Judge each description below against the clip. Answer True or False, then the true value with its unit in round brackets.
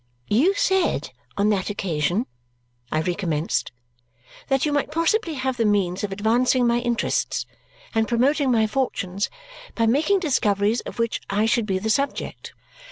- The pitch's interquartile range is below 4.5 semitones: False (5.0 semitones)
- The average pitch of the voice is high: True (230 Hz)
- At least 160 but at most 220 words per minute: False (150 wpm)